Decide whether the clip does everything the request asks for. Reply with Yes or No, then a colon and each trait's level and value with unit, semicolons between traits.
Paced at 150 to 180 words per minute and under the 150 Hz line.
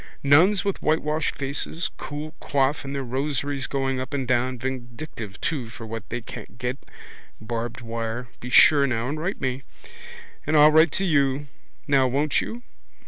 Yes: average, 170 wpm; low, 135 Hz